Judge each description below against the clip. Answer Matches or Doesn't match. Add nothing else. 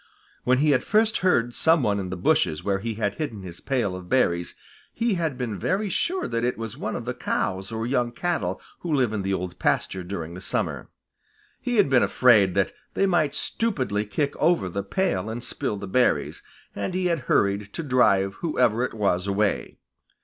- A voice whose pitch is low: Matches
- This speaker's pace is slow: Doesn't match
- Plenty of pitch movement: Matches